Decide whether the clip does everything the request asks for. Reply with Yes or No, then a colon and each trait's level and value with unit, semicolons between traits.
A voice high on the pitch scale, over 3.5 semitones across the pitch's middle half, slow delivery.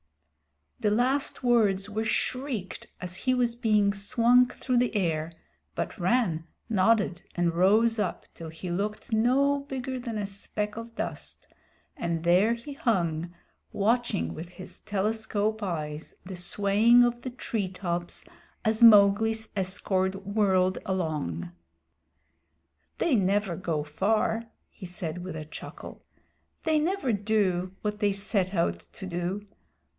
Yes: high, 205 Hz; average, 4.1 semitones; slow, 130 wpm